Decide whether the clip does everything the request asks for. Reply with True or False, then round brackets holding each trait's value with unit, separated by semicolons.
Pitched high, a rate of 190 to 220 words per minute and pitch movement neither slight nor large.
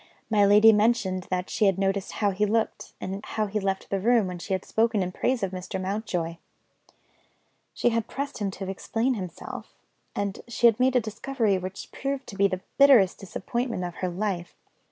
True (200 Hz; 195 wpm; 3.4 semitones)